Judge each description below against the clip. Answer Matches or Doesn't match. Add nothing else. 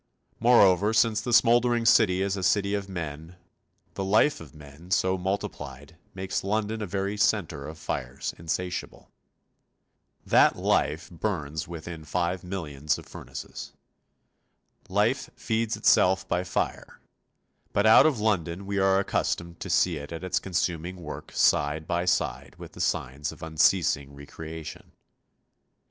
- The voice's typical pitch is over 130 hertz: Doesn't match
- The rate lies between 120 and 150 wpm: Matches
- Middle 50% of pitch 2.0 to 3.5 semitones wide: Doesn't match